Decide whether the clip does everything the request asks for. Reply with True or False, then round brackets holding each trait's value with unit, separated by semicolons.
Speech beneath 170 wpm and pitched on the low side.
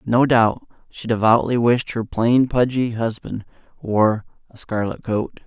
True (145 wpm; 115 Hz)